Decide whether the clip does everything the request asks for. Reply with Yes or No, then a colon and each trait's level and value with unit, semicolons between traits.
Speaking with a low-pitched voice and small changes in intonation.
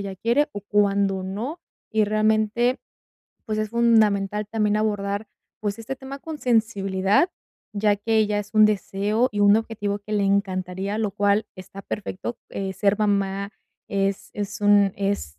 No: high, 205 Hz; narrow, 1.7 semitones